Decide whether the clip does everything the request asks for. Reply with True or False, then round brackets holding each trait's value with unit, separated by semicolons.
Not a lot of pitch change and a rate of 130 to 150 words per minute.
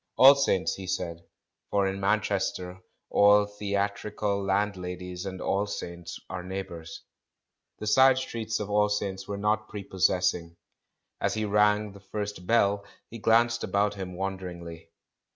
True (2.1 semitones; 145 wpm)